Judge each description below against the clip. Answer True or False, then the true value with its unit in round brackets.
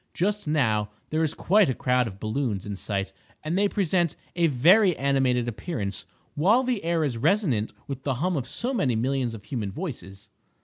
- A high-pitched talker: False (140 Hz)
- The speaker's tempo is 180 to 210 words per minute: True (185 wpm)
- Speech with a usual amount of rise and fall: False (7.4 semitones)